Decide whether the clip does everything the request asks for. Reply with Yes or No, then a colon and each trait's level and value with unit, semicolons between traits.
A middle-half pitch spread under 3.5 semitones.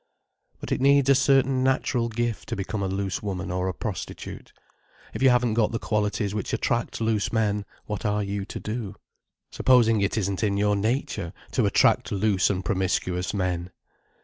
Yes: average, 3.1 semitones